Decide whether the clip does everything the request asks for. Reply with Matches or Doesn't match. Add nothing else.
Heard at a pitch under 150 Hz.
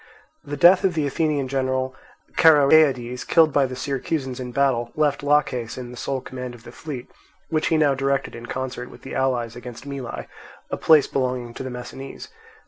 Matches